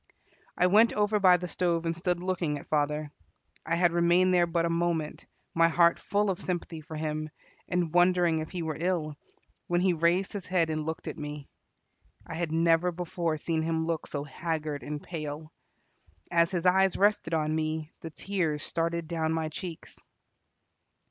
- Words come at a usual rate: Yes, average, 180 wpm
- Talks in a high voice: No, medium, 165 Hz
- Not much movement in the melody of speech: Yes, narrow, 2.2 semitones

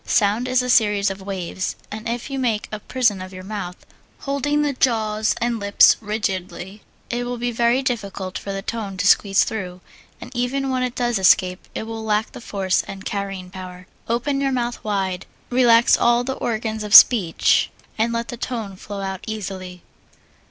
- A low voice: No, high, 215 Hz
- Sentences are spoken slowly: No, average, 180 wpm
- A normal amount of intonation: Yes, average, 3.8 semitones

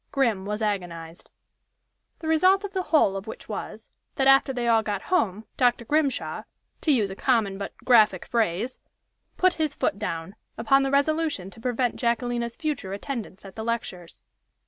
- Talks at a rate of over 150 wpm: Yes, average, 170 wpm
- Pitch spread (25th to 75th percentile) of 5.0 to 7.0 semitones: Yes, wide, 5.6 semitones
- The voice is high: Yes, high, 235 Hz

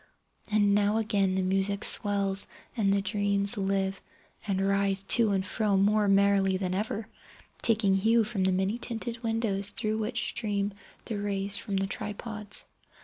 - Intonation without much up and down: Yes, narrow, 1.7 semitones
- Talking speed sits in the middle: Yes, average, 155 wpm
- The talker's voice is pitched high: Yes, high, 200 Hz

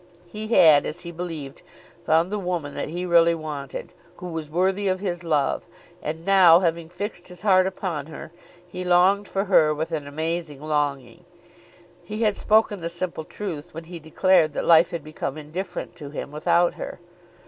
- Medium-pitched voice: Yes, medium, 170 Hz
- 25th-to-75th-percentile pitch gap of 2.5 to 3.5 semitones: Yes, average, 3.0 semitones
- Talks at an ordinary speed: Yes, average, 180 wpm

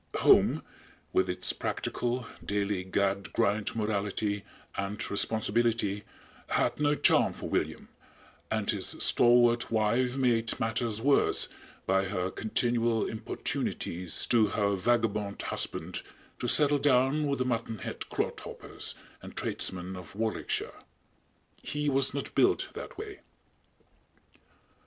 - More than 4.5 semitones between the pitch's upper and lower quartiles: No, average, 3.4 semitones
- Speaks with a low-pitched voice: Yes, low, 110 Hz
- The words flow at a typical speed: No, slow, 115 wpm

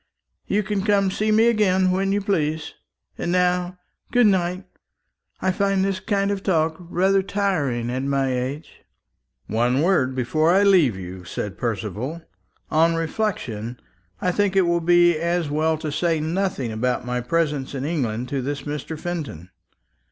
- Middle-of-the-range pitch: Yes, medium, 165 Hz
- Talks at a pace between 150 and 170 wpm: Yes, average, 160 wpm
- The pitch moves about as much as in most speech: No, wide, 6.3 semitones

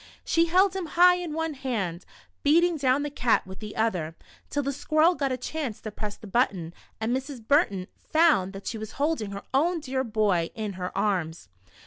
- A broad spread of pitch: Yes, wide, 7.5 semitones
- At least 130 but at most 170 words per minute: No, average, 200 wpm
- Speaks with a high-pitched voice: Yes, very high, 255 Hz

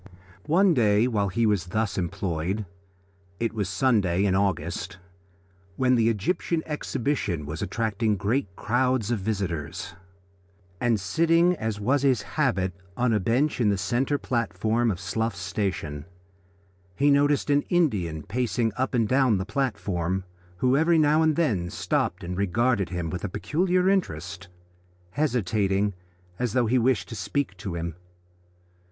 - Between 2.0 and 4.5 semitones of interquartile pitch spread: No, wide, 5.6 semitones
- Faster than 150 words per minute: No, average, 145 wpm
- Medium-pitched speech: No, low, 110 Hz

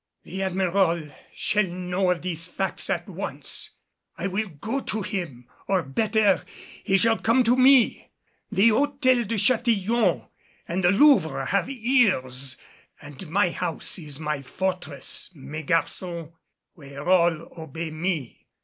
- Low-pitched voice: No, medium, 185 Hz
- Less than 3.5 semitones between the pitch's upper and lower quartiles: No, average, 5.3 semitones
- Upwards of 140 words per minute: No, slow, 135 wpm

